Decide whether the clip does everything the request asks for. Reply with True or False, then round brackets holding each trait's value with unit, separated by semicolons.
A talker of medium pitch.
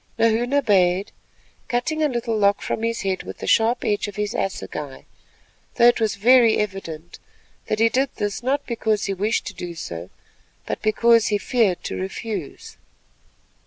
False (215 Hz)